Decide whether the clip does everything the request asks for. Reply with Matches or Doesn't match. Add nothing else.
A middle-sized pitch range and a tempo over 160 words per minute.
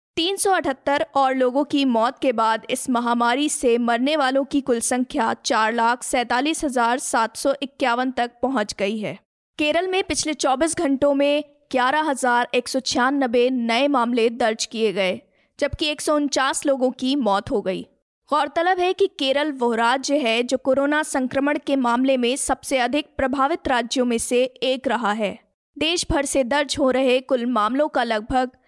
Matches